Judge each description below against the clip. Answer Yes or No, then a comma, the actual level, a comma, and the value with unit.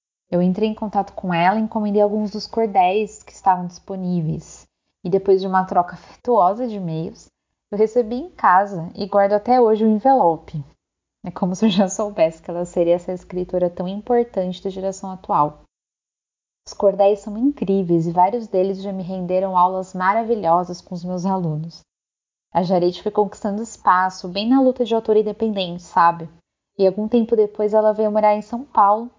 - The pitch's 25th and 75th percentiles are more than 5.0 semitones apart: No, average, 3.1 semitones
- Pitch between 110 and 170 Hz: No, high, 195 Hz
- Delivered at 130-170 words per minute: No, average, 180 wpm